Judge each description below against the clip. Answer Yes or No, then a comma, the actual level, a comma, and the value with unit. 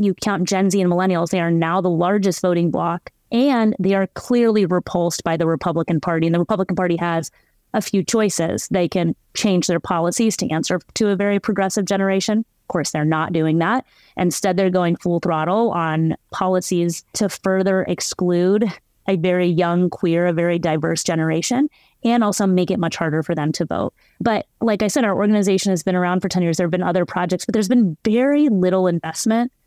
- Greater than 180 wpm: Yes, average, 200 wpm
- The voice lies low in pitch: No, medium, 180 Hz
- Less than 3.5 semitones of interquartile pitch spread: Yes, average, 2.9 semitones